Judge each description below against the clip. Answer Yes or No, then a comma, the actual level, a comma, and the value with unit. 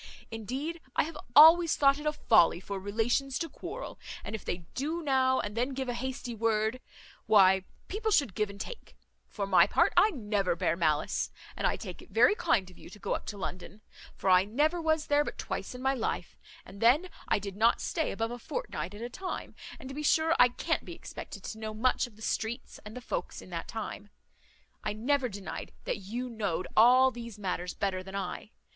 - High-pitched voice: Yes, high, 235 Hz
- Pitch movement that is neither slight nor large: No, wide, 5.7 semitones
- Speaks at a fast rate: Yes, fast, 215 wpm